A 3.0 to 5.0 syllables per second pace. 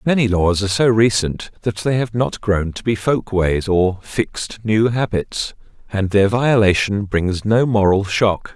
Yes: 4.2 syllables/s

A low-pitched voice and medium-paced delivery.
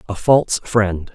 Yes: low, 105 Hz; average, 160 wpm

